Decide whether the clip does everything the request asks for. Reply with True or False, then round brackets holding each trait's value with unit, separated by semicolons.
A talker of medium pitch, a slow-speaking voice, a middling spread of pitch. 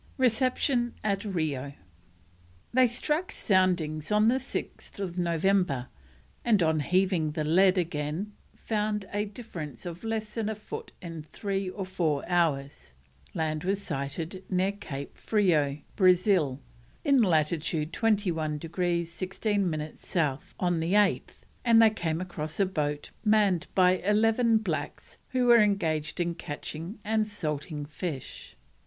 True (180 Hz; 130 wpm; 5.0 semitones)